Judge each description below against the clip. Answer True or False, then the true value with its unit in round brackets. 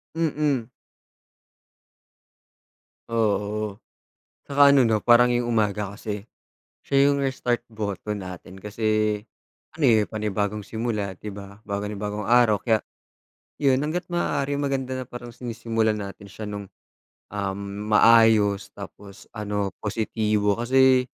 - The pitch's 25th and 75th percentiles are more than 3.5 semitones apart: False (3.1 semitones)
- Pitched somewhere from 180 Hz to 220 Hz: False (110 Hz)